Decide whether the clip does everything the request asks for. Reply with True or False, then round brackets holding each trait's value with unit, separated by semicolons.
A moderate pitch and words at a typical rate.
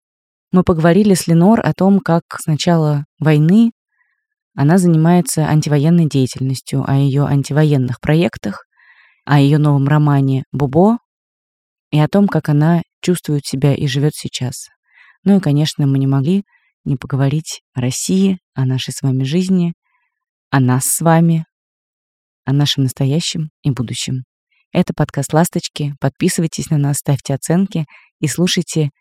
True (150 Hz; 140 wpm)